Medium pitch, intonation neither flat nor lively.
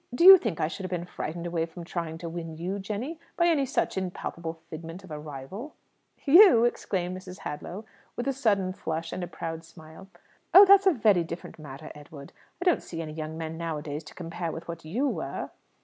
Yes: medium, 175 Hz; average, 4.9 semitones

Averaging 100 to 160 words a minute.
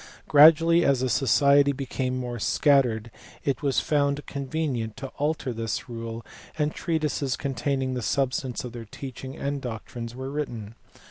Yes: average, 150 wpm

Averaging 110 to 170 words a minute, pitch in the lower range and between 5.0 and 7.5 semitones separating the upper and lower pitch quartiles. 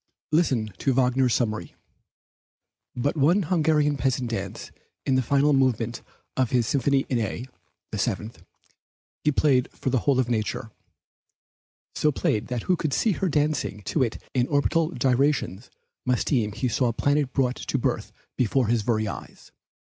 No: average, 160 wpm; low, 130 Hz; average, 3.5 semitones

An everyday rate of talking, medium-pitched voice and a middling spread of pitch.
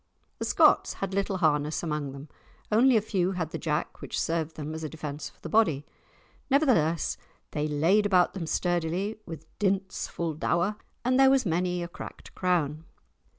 Yes: average, 175 wpm; medium, 170 Hz; average, 4.1 semitones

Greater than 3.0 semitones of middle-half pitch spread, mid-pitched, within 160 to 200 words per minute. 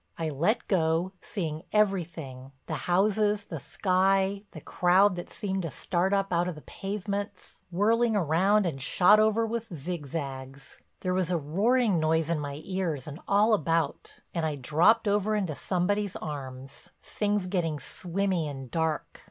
No: average, 4.4 semitones; medium, 180 Hz; average, 150 wpm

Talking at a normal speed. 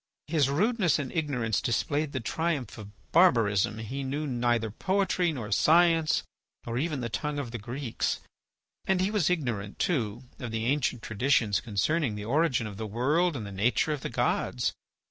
Yes: average, 170 wpm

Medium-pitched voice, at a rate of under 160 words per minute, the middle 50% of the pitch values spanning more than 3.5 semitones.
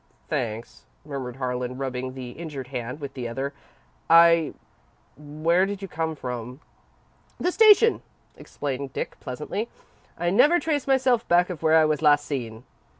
Yes: medium, 150 Hz; average, 150 wpm; average, 5.3 semitones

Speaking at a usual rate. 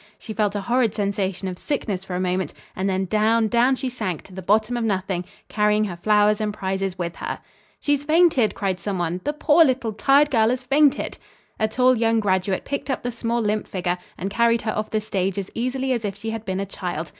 No: fast, 225 wpm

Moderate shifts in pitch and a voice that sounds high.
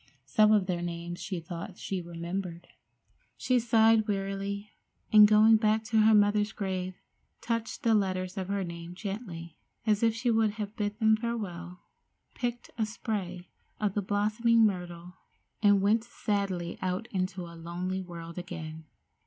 Yes: average, 3.5 semitones; high, 200 Hz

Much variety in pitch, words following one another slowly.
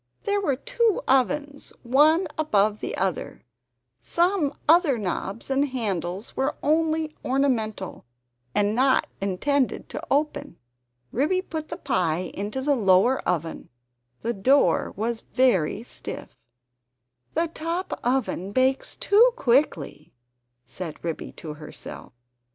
Yes: wide, 7.4 semitones; slow, 115 wpm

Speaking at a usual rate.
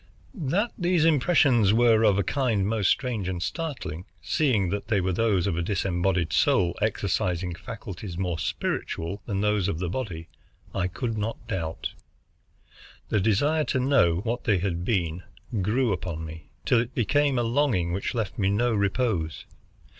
Yes: average, 160 wpm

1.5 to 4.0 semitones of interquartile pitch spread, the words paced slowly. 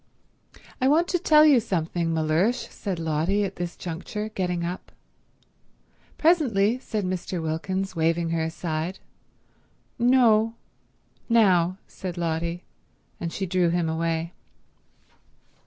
No: average, 4.5 semitones; slow, 110 wpm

